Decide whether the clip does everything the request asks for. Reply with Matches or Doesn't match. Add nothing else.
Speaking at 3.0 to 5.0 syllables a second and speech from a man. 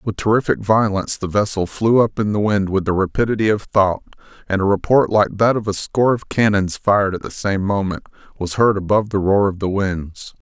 Doesn't match